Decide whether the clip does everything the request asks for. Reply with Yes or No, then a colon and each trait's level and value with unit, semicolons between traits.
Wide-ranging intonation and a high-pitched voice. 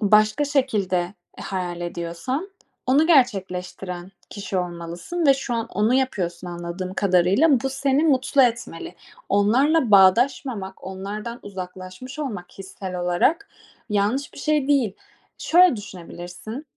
Yes: wide, 6.6 semitones; high, 210 Hz